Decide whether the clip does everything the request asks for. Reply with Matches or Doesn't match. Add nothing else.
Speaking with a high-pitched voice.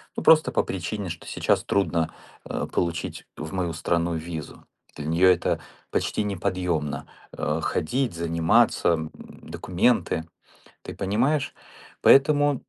Doesn't match